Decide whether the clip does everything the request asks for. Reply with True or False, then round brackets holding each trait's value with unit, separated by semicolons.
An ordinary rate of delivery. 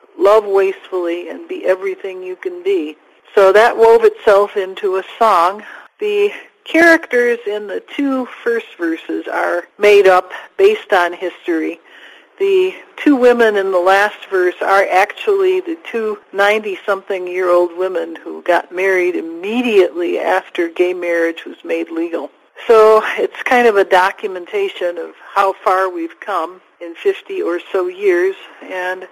True (145 wpm)